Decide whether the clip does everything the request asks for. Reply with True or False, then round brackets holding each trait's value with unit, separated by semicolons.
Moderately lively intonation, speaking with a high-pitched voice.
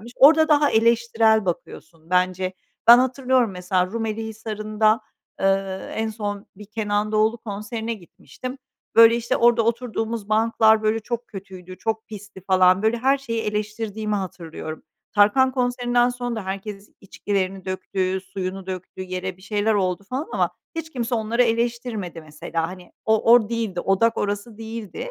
True (3.4 semitones; 215 Hz)